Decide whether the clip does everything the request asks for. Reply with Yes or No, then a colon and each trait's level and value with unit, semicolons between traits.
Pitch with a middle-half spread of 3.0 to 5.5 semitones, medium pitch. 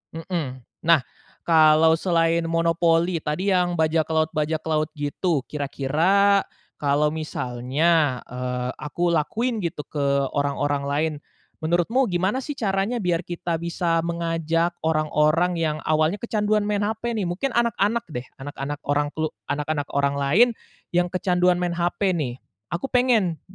Yes: average, 3.3 semitones; medium, 165 Hz